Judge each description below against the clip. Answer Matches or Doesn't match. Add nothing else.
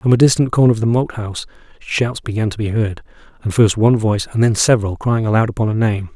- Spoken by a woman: Doesn't match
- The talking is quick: Matches